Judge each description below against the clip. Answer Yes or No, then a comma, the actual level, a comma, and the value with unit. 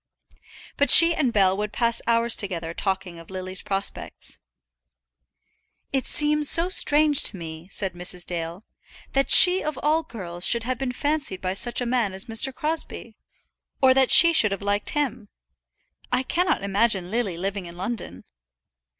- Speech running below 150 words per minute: No, average, 160 wpm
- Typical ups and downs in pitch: No, wide, 6.3 semitones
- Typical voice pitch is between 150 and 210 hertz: No, high, 225 Hz